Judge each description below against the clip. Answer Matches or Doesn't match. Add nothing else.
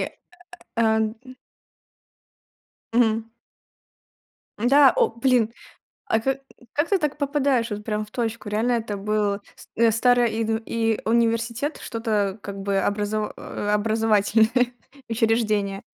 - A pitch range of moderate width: Doesn't match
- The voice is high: Matches